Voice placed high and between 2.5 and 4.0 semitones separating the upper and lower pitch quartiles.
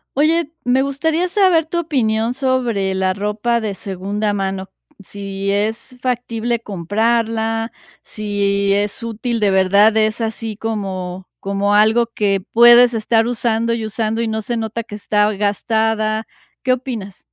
Yes: high, 220 Hz; average, 2.8 semitones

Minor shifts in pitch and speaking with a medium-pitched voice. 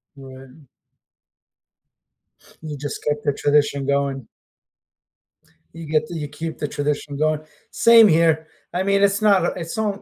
No: average, 3.3 semitones; medium, 155 Hz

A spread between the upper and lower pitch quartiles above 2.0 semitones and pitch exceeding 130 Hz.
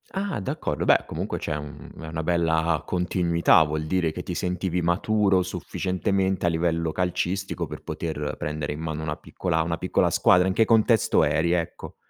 No: narrow, 2.5 semitones; very low, 85 Hz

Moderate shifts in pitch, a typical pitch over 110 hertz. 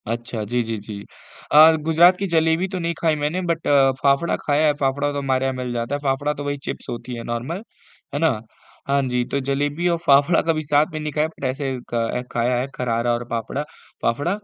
Yes: average, 4.4 semitones; medium, 140 Hz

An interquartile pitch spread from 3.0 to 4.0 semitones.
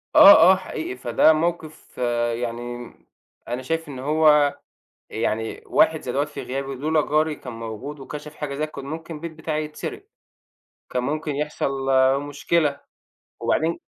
Yes: average, 3.3 semitones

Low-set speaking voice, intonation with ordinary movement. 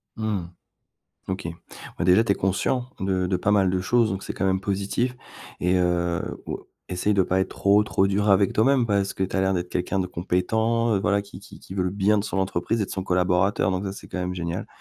No: very low, 95 Hz; narrow, 2.0 semitones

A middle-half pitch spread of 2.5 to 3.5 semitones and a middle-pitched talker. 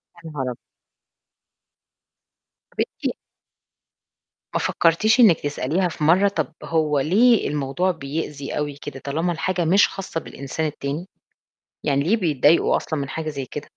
No: average, 3.9 semitones; medium, 160 Hz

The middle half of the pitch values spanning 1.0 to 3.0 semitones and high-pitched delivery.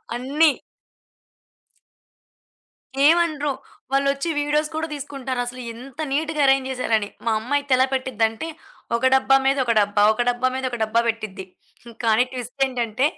No: average, 3.4 semitones; very high, 260 Hz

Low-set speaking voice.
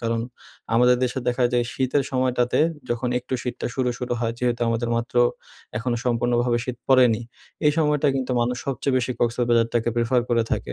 Yes: low, 125 Hz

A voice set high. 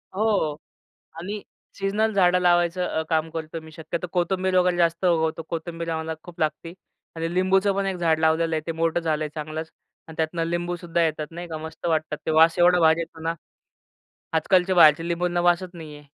No: medium, 170 Hz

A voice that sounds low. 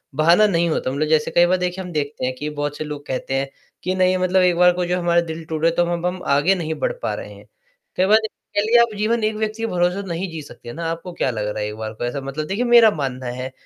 No: medium, 170 Hz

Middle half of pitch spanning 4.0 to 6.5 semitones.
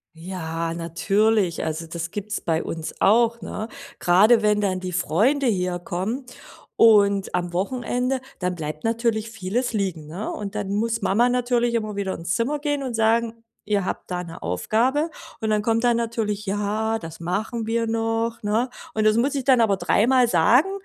Yes: average, 4.3 semitones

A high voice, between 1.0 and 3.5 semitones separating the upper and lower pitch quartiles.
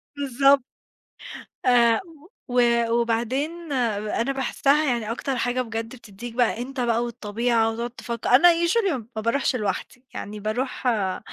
Yes: high, 240 Hz; average, 2.8 semitones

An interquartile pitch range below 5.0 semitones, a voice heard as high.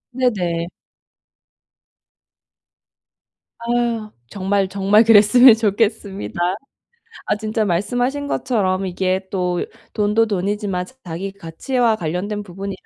Yes: average, 3.2 semitones; high, 205 Hz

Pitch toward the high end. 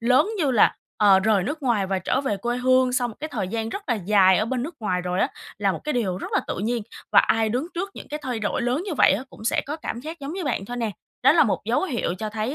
Yes: high, 240 Hz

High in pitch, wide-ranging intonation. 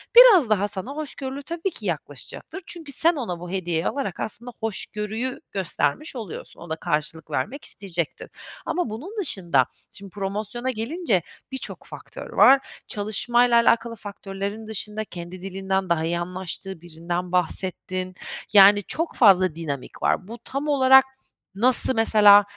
Yes: high, 205 Hz; wide, 5.7 semitones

